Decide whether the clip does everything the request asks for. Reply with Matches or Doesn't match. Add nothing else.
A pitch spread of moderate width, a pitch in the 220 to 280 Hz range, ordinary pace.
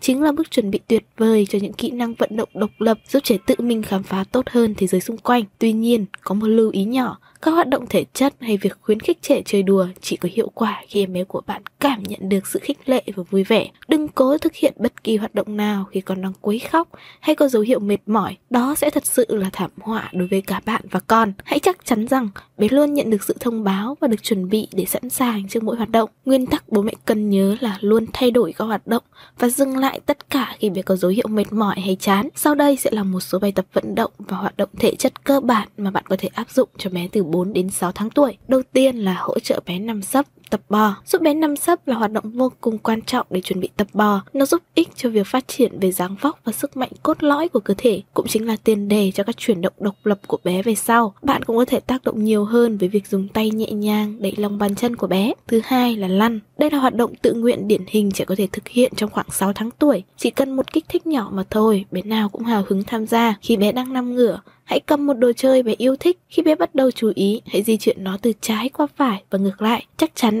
Doesn't match